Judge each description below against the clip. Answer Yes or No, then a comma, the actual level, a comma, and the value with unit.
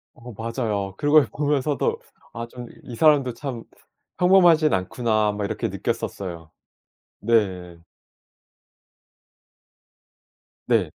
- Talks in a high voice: No, low, 115 Hz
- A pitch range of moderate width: No, wide, 5.9 semitones